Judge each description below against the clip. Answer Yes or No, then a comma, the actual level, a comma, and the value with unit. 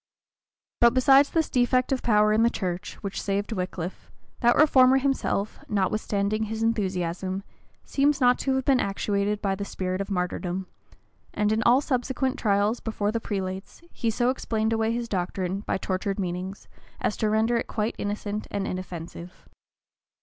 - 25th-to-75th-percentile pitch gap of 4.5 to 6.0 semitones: No, average, 3.8 semitones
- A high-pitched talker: Yes, high, 210 Hz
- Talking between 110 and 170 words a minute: Yes, average, 160 wpm